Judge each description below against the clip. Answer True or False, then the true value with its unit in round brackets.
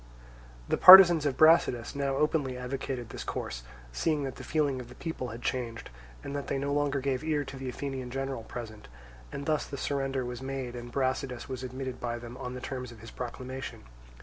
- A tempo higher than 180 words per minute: True (200 wpm)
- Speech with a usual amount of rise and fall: False (2.2 semitones)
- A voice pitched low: True (130 Hz)